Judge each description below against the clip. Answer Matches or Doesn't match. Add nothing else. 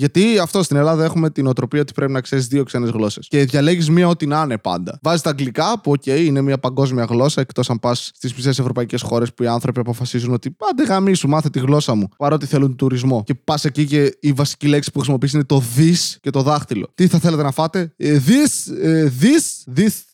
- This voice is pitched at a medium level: Matches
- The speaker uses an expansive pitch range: Doesn't match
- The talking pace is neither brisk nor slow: Doesn't match